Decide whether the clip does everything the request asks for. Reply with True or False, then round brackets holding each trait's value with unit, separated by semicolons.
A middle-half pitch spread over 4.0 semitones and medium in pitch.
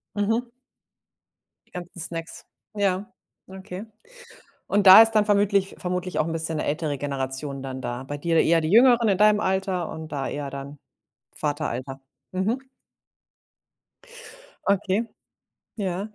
True (5.6 semitones; 180 Hz)